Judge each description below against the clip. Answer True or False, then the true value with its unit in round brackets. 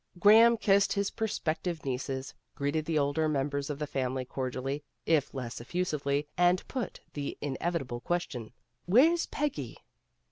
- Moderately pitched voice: True (150 Hz)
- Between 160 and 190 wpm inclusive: False (145 wpm)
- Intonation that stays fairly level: False (5.1 semitones)